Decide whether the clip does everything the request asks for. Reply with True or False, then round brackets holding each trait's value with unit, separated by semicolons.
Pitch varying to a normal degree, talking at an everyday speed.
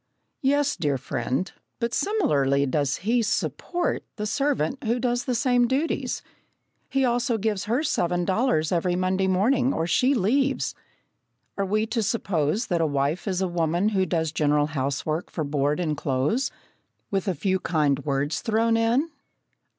False (7.8 semitones; 160 wpm)